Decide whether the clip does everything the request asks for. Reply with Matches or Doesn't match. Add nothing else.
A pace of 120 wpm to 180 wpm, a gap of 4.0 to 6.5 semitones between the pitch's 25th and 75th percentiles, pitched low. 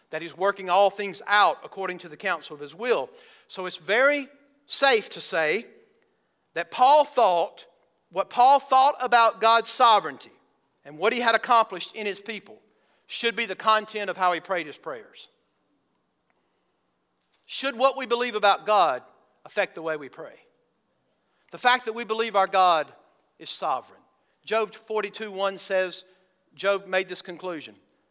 Doesn't match